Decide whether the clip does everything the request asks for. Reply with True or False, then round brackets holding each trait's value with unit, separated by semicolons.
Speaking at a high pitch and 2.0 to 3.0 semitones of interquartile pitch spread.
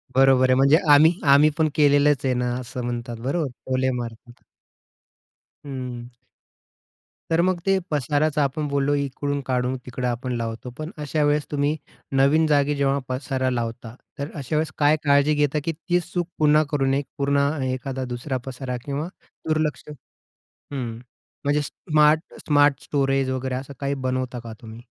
False (140 Hz; 2.5 semitones)